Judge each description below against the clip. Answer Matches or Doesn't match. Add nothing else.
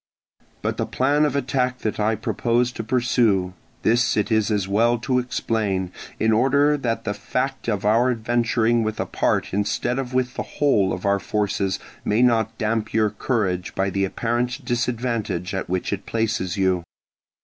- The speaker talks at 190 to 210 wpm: Doesn't match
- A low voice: Matches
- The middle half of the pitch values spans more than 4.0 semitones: Doesn't match